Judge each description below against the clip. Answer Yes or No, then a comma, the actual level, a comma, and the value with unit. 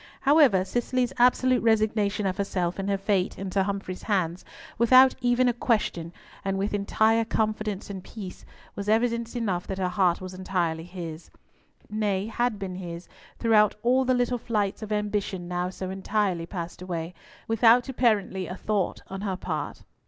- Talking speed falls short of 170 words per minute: Yes, average, 160 wpm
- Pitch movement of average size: Yes, average, 3.5 semitones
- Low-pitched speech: No, high, 200 Hz